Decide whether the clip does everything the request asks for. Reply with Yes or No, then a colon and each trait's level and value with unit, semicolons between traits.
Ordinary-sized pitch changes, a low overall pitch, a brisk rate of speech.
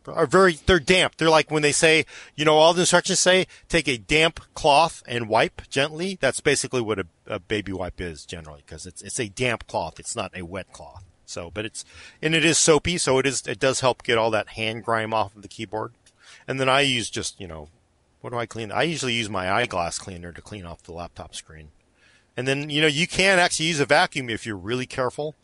No: wide, 7.6 semitones; low, 120 Hz; fast, 240 wpm